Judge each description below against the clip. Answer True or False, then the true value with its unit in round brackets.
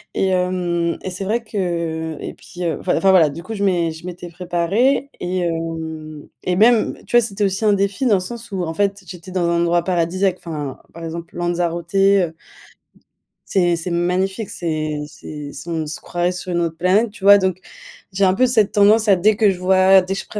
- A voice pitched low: False (180 Hz)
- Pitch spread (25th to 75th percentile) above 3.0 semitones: False (2.7 semitones)